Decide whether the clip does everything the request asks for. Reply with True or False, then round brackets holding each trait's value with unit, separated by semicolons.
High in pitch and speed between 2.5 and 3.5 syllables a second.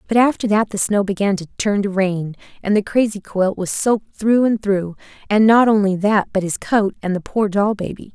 False (205 Hz; 5.1 syllables/s)